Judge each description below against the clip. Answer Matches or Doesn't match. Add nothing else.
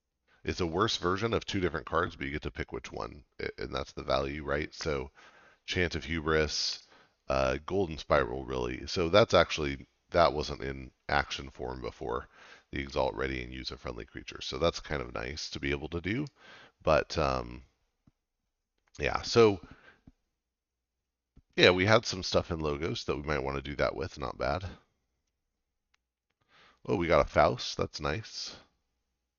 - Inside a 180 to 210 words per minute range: Doesn't match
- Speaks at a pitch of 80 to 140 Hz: Doesn't match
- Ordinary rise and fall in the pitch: Matches